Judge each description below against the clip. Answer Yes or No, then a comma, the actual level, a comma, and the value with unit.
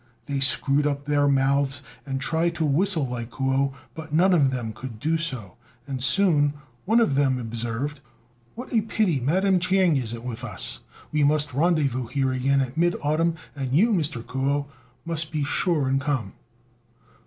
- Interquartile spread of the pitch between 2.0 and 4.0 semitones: Yes, average, 3.6 semitones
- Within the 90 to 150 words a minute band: No, average, 170 wpm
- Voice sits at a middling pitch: Yes, medium, 145 Hz